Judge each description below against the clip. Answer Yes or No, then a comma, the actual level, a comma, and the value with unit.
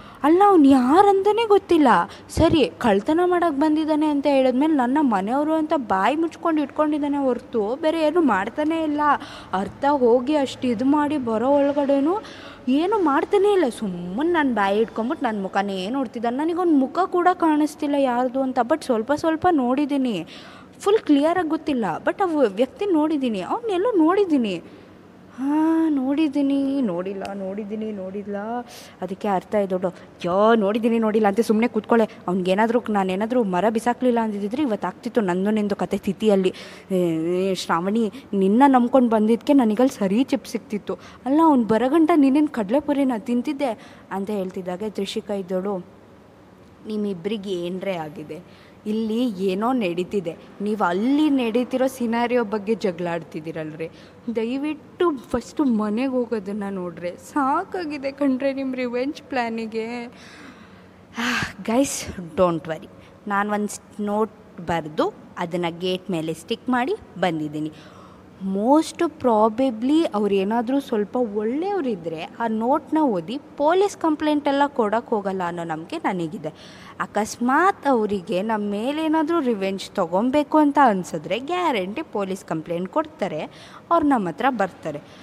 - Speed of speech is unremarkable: No, fast, 120 wpm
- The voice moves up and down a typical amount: No, wide, 6.7 semitones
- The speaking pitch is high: Yes, high, 240 Hz